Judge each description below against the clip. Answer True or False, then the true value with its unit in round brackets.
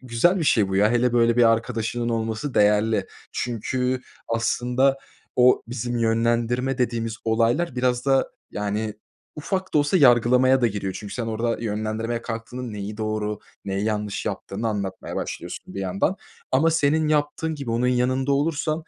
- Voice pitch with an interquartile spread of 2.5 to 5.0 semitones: True (3.0 semitones)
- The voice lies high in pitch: False (120 Hz)